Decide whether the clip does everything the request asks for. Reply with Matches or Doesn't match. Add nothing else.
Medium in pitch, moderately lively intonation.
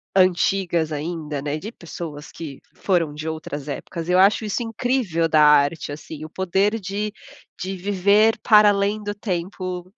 Matches